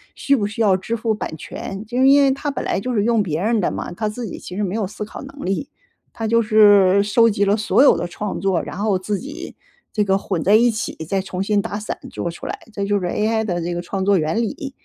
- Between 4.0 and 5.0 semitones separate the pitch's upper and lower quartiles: No, average, 2.8 semitones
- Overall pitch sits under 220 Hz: Yes, high, 210 Hz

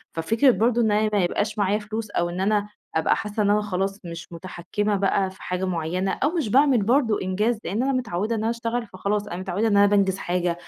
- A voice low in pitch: No, high, 205 Hz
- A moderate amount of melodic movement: Yes, average, 3.0 semitones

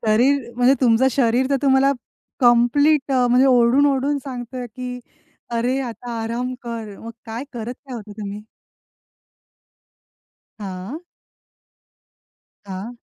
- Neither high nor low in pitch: No, high, 245 Hz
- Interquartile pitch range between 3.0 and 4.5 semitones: No, narrow, 2.5 semitones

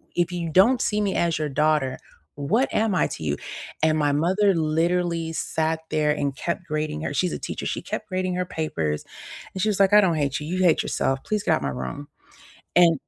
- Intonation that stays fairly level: No, average, 3.5 semitones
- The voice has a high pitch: No, medium, 165 Hz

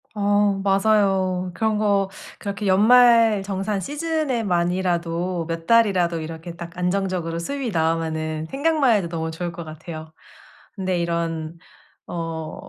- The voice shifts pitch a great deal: No, average, 3.8 semitones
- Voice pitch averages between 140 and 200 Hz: Yes, medium, 185 Hz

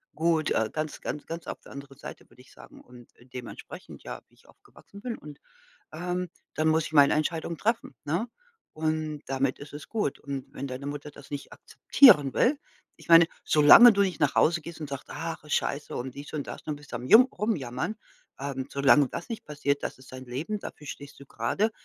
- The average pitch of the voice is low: No, medium, 150 Hz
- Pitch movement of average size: Yes, average, 3.3 semitones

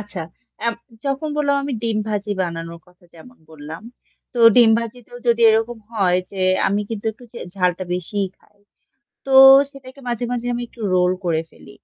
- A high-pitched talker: Yes, high, 210 Hz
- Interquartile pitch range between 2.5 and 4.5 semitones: No, average, 5.2 semitones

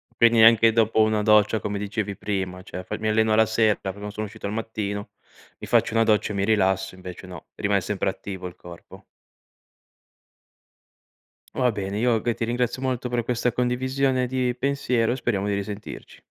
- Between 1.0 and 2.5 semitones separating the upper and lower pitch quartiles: No, average, 2.9 semitones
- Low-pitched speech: Yes, low, 110 Hz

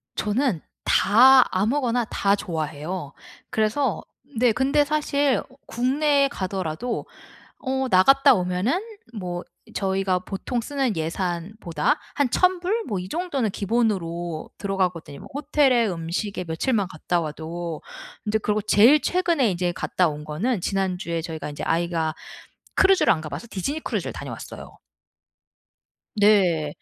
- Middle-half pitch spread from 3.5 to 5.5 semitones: No, wide, 7.2 semitones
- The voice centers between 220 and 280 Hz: No, high, 200 Hz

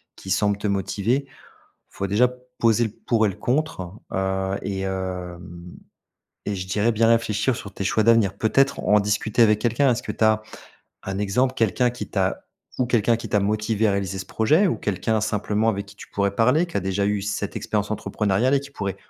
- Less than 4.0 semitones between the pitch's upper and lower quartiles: Yes, average, 2.9 semitones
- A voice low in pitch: Yes, low, 105 Hz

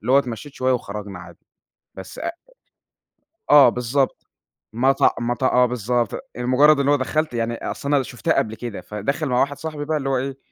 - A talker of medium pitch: No, low, 130 Hz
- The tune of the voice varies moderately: Yes, average, 3.1 semitones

